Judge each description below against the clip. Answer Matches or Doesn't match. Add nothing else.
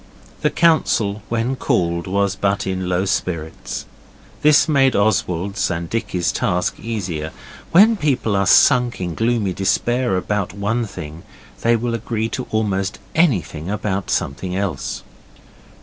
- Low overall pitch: Matches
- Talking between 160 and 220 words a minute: Doesn't match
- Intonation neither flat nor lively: Matches